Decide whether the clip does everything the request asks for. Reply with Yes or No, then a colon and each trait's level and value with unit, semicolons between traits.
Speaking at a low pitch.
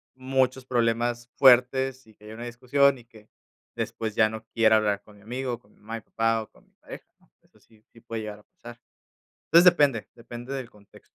Yes: low, 120 Hz